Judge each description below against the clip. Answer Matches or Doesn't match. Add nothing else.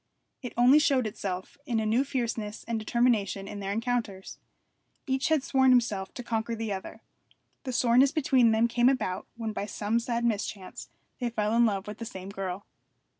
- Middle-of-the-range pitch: Doesn't match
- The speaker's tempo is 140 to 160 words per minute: Doesn't match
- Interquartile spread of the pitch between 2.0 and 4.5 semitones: Matches